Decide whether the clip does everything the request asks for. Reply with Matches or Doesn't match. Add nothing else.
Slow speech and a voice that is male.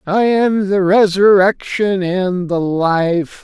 Matches